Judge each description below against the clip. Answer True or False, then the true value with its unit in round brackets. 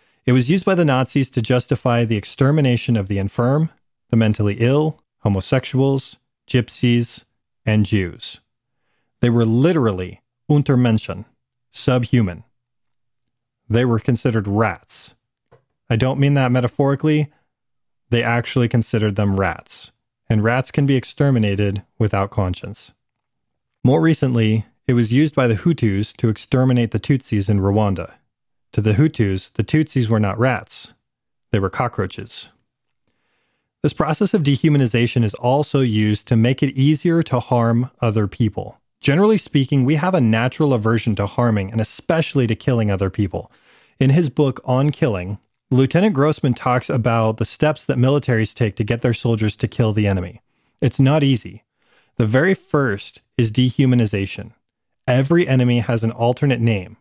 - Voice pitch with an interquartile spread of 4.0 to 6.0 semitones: False (3.6 semitones)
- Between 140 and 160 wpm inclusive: True (145 wpm)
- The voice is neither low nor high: False (120 Hz)